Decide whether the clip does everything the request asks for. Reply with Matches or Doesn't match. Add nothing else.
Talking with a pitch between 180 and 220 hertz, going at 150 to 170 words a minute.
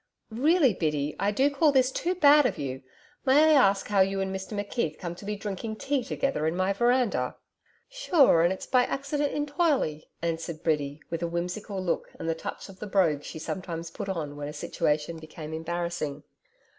Doesn't match